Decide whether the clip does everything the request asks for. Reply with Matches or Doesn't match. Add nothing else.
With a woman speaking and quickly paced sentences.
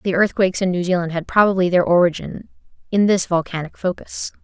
Doesn't match